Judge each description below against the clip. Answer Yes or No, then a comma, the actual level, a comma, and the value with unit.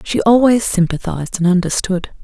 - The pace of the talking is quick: No, slow, 135 wpm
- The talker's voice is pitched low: No, high, 195 Hz